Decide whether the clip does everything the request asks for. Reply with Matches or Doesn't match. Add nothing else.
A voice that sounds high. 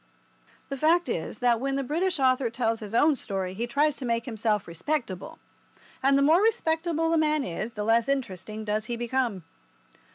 Matches